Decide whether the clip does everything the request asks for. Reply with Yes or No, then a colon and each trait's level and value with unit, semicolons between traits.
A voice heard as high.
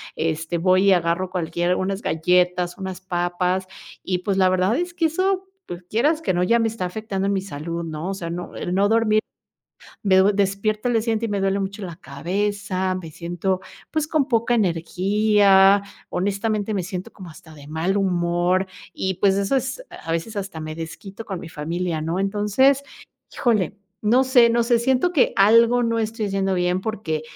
Yes: high, 195 Hz